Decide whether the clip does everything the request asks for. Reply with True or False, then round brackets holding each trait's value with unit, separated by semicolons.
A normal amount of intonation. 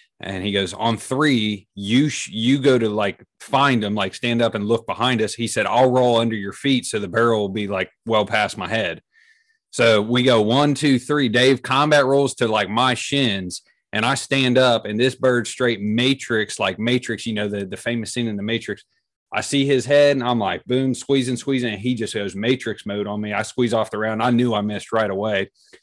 True (3.3 semitones)